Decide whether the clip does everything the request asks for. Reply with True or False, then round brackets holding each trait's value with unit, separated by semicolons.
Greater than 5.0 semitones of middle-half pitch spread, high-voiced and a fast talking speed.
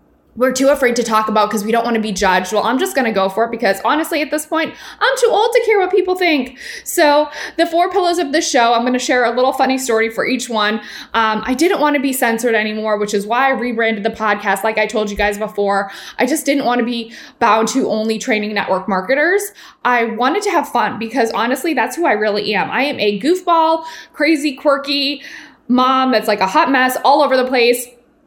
True (5.4 semitones; 250 Hz; 240 wpm)